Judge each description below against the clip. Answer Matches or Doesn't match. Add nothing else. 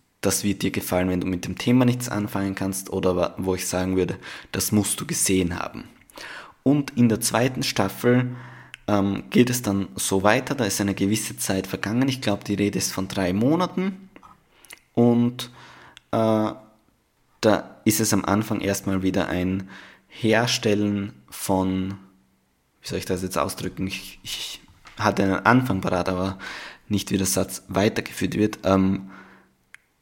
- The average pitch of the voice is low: Matches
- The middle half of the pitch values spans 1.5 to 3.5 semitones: Matches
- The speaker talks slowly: Doesn't match